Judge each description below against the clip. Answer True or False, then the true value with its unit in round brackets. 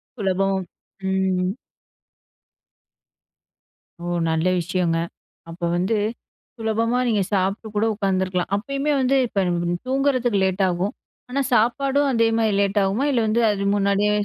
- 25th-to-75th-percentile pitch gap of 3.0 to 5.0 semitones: True (3.7 semitones)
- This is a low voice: False (205 Hz)